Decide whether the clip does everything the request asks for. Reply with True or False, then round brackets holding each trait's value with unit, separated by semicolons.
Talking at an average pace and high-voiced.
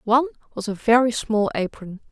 True (170 wpm; 230 Hz)